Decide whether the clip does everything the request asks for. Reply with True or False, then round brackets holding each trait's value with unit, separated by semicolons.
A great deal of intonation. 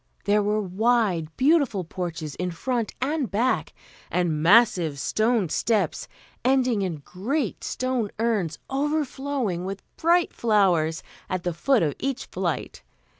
True (6.3 semitones)